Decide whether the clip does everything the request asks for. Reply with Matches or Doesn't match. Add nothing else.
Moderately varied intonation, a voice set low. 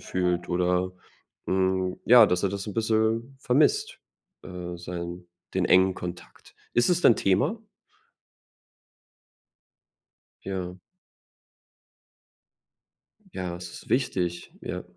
Matches